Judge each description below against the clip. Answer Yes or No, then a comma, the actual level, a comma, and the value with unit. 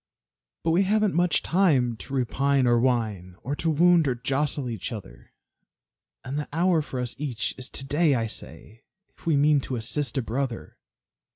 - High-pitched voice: No, low, 135 Hz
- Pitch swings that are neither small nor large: Yes, average, 4.4 semitones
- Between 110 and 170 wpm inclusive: No, average, 180 wpm